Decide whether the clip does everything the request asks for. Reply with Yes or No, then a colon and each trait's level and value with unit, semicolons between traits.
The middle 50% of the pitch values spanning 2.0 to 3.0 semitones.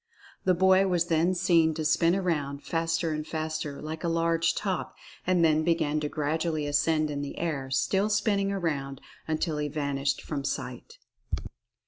Yes: narrow, 2.6 semitones